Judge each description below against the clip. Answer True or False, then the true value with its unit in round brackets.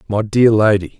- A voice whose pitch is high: False (105 Hz)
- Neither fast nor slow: True (180 wpm)